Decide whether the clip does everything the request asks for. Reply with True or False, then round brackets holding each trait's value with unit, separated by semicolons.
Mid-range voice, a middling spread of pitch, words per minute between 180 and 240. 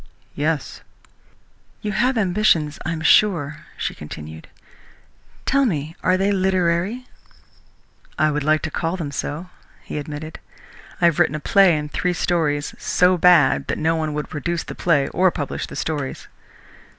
False (165 Hz; 3.7 semitones; 155 wpm)